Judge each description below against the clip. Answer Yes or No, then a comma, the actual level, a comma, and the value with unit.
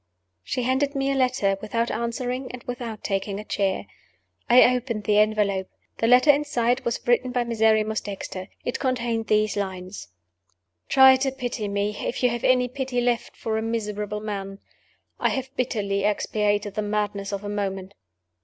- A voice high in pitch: Yes, high, 225 Hz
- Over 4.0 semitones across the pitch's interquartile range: No, average, 3.4 semitones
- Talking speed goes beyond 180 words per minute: No, average, 165 wpm